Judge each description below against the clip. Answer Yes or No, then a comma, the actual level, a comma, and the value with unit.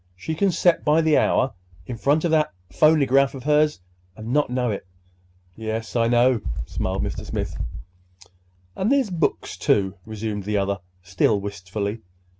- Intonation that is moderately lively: No, wide, 6.8 semitones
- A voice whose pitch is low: Yes, low, 120 Hz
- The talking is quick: No, average, 155 wpm